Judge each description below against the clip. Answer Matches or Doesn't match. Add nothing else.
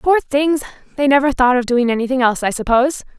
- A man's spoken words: Doesn't match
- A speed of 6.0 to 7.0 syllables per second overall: Matches